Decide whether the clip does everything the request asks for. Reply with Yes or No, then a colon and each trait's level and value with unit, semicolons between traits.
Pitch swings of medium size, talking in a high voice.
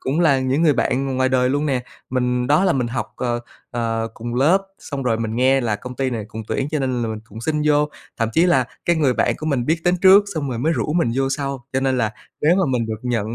No: average, 3.8 semitones; low, 130 Hz